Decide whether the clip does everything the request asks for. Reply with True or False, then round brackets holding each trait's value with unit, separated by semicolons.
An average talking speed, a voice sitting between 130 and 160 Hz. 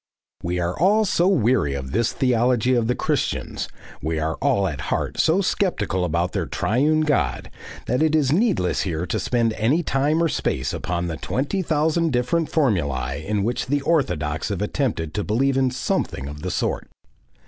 False (180 wpm; 120 Hz)